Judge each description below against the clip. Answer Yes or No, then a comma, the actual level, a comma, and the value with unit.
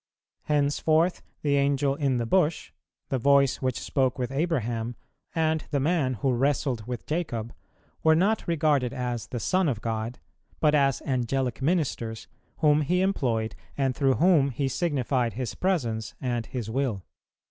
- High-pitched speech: No, low, 135 Hz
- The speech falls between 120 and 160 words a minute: Yes, average, 150 wpm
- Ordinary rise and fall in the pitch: Yes, average, 3.9 semitones